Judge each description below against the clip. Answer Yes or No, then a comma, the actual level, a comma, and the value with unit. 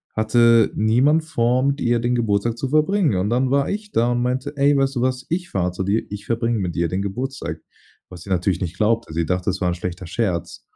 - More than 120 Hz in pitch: No, low, 115 Hz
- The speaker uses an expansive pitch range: Yes, wide, 5.8 semitones